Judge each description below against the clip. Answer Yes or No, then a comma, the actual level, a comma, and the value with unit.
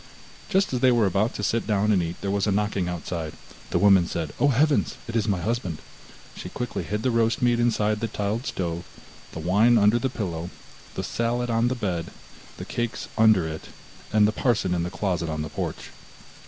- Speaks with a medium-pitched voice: No, low, 105 Hz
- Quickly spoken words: Yes, fast, 210 wpm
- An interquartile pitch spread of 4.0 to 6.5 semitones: Yes, average, 4.7 semitones